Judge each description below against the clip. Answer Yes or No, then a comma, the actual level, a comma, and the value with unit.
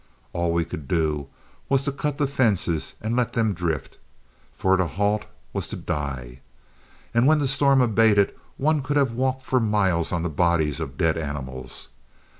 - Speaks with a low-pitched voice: Yes, low, 100 Hz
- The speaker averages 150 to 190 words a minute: Yes, average, 175 wpm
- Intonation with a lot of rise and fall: Yes, wide, 8.5 semitones